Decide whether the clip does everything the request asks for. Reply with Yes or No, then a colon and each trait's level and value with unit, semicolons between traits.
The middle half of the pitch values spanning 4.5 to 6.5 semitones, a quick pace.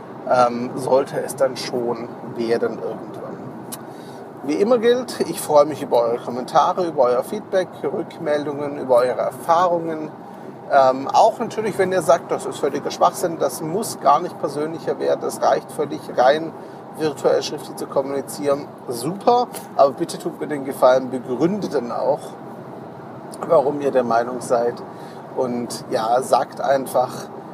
No: average, 5.3 semitones; average, 145 wpm